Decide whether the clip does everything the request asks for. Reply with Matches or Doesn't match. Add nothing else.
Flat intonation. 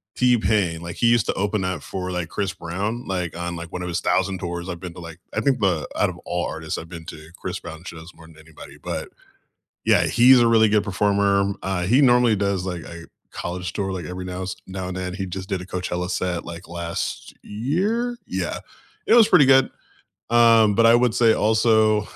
Doesn't match